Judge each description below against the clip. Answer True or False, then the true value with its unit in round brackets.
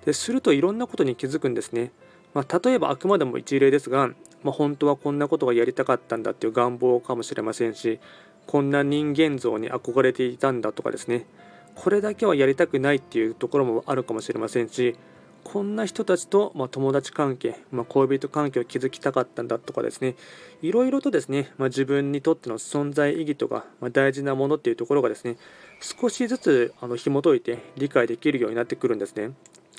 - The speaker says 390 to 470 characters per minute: True (430 characters per minute)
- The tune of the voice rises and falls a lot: False (4.6 semitones)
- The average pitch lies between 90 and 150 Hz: True (140 Hz)